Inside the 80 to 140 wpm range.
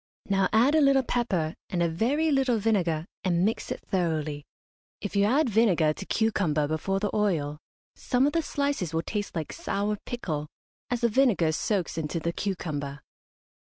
No: average, 170 wpm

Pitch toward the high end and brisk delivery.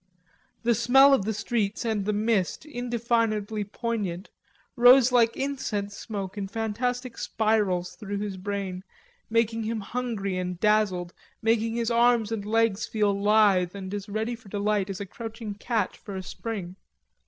No: high, 215 Hz; average, 155 wpm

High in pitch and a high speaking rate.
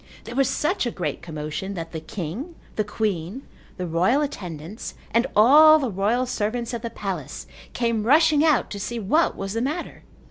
No: high, 225 Hz; average, 180 wpm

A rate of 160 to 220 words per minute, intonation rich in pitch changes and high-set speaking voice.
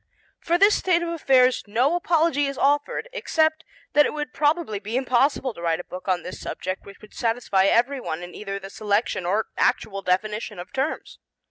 Yes: average, 190 wpm; wide, 7.0 semitones; high, 245 Hz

